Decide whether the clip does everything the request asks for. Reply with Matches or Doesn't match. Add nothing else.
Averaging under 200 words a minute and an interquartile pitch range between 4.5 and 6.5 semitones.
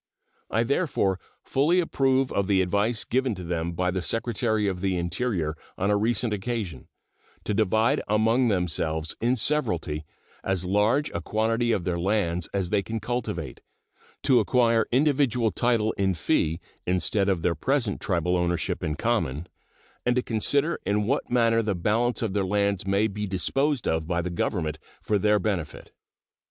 Matches